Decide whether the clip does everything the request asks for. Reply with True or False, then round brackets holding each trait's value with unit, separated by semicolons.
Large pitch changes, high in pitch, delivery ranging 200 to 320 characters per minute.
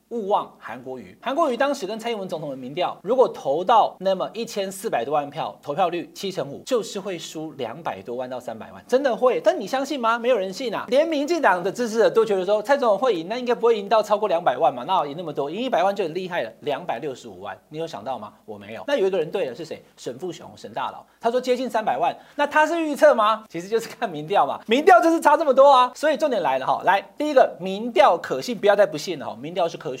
False (6.7 semitones; 230 Hz; 385 characters per minute)